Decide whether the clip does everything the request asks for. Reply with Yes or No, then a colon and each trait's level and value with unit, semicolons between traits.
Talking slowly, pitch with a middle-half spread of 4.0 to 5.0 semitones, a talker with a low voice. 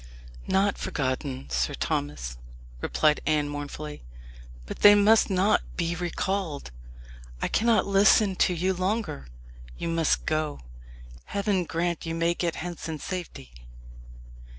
No: slow, 125 wpm; average, 4.7 semitones; medium, 170 Hz